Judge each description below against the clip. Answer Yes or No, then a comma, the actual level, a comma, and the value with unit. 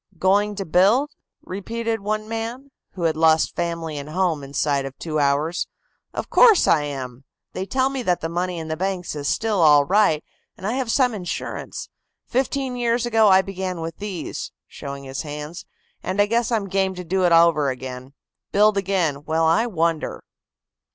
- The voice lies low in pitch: No, medium, 180 Hz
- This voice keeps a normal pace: Yes, average, 180 wpm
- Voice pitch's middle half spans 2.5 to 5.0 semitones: No, wide, 5.4 semitones